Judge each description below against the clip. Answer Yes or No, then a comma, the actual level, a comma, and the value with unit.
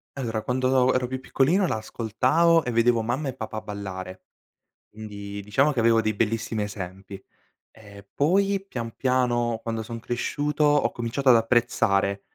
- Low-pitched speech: Yes, low, 115 Hz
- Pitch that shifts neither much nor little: Yes, average, 3.5 semitones